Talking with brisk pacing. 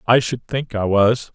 Yes: fast, 225 wpm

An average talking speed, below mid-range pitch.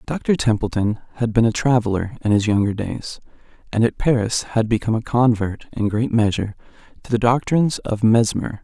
Yes: average, 175 wpm; low, 110 Hz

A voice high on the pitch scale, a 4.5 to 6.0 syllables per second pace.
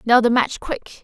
Yes: high, 240 Hz; 5.6 syllables/s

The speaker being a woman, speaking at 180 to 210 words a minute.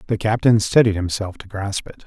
No: male; fast, 205 wpm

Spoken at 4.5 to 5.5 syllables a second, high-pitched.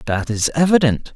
No: 5.1 syllables/s; medium, 140 Hz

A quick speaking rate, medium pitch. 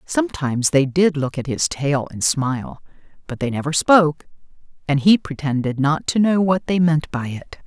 No: average, 190 wpm; medium, 150 Hz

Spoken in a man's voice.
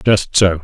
Yes: male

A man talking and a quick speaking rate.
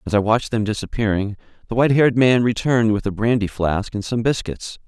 Yes: male; fast, 210 wpm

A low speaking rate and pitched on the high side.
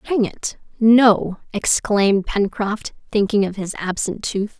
Yes: slow, 130 wpm; high, 210 Hz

